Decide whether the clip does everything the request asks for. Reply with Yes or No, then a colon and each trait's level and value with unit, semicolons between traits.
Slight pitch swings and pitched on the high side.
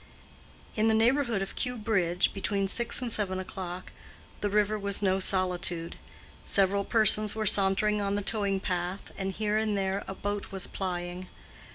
Yes: narrow, 2.1 semitones; high, 200 Hz